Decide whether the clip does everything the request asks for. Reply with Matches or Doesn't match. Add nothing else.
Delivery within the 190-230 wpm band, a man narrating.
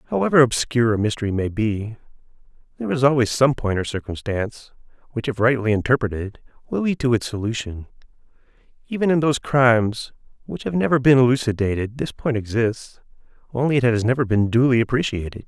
Doesn't match